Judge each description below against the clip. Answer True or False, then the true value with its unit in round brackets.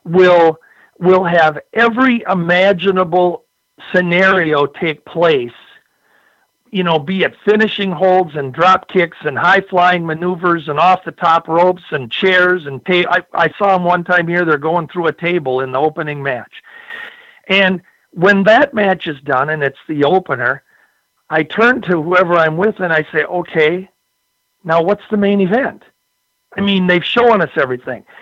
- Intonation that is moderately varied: True (3.0 semitones)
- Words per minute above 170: False (165 wpm)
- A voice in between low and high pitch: True (180 Hz)